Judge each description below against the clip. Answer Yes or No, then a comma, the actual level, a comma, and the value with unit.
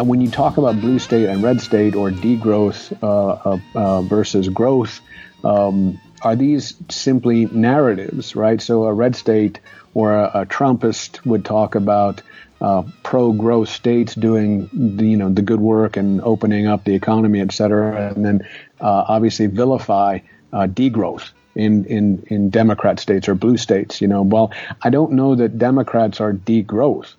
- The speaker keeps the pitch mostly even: Yes, narrow, 2.3 semitones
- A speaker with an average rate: Yes, average, 170 wpm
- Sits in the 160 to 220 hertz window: No, low, 110 Hz